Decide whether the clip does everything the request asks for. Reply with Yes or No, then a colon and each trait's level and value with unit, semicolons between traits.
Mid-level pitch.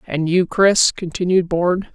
Yes: medium, 175 Hz